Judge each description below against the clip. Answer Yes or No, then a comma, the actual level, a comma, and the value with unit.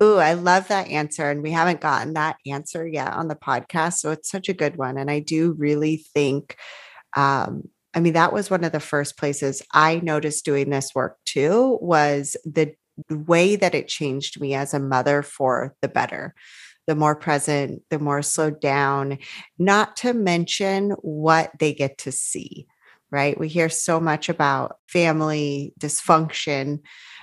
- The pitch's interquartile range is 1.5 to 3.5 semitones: Yes, narrow, 2.4 semitones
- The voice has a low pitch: No, medium, 155 Hz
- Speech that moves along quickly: No, average, 170 wpm